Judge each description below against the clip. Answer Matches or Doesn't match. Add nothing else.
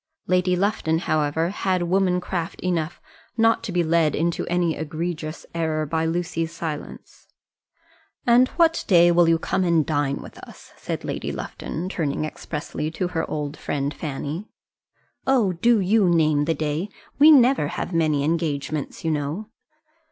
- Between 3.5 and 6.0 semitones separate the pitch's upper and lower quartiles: Doesn't match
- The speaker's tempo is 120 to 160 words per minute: Matches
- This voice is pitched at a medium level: Matches